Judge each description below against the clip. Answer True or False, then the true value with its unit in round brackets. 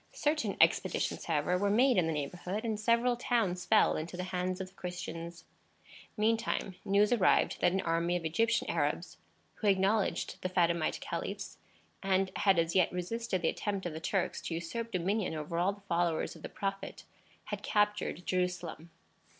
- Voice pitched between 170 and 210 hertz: True (185 Hz)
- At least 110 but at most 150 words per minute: False (170 wpm)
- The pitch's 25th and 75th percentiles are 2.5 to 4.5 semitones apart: True (3.4 semitones)